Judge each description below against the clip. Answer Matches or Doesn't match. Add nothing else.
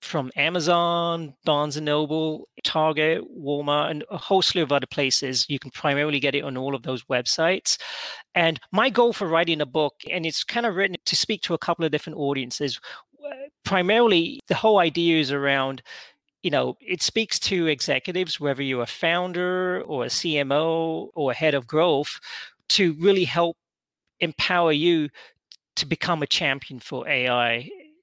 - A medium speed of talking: Matches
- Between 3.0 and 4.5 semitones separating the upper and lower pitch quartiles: Matches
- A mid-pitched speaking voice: Matches